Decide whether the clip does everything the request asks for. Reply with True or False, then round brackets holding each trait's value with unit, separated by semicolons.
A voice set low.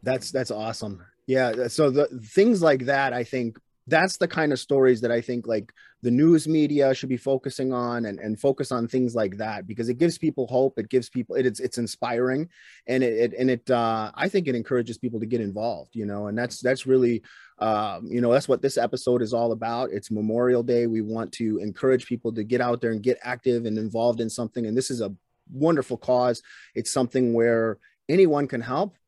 True (125 Hz)